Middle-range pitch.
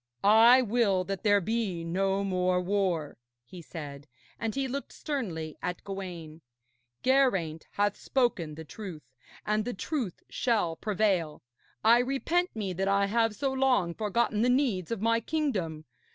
No: high, 200 Hz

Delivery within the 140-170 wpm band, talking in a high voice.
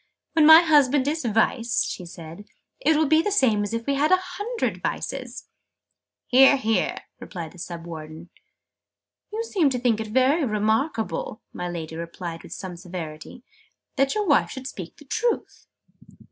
Yes: average, 165 wpm; high, 245 Hz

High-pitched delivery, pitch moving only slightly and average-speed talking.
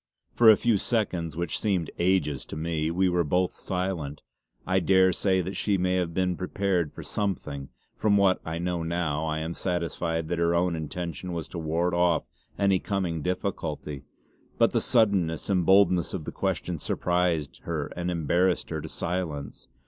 No: very low, 90 Hz; narrow, 2.3 semitones; average, 170 wpm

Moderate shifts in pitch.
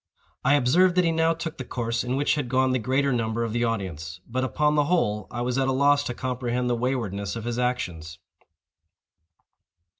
Yes: average, 3.4 semitones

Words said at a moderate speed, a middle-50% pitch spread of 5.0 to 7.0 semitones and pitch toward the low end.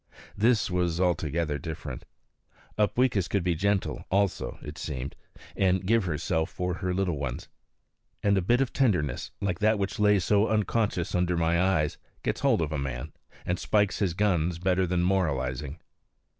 No: average, 160 wpm; average, 3.8 semitones; very low, 90 Hz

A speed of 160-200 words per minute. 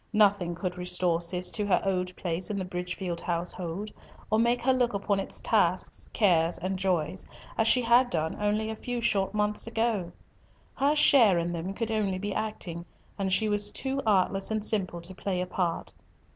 Yes: average, 185 wpm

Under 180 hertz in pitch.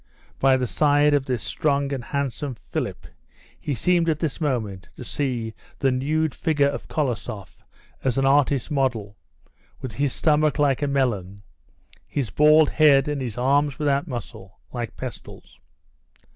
Yes: low, 135 Hz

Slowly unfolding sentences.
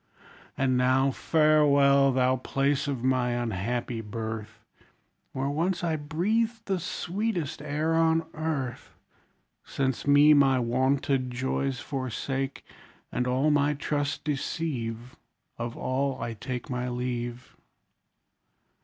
Yes: slow, 110 wpm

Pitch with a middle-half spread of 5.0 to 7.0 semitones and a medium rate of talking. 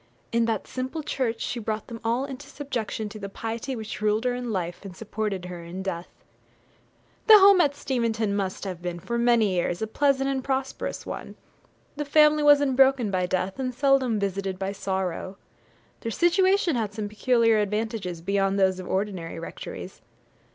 Yes: average, 5.3 semitones; average, 175 wpm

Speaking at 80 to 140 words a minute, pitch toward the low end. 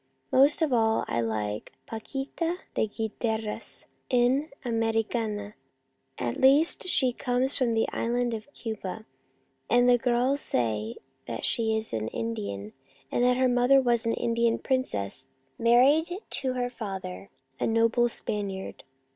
No: slow, 135 wpm; high, 230 Hz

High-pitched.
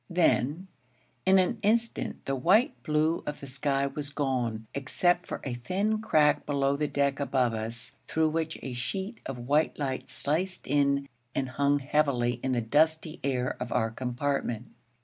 No: medium, 140 Hz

